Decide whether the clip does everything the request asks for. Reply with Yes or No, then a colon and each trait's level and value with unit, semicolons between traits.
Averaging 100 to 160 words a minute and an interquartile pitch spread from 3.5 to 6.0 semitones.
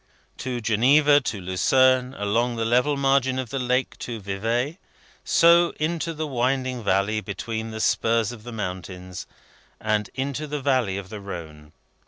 Yes: average, 155 wpm; average, 4.4 semitones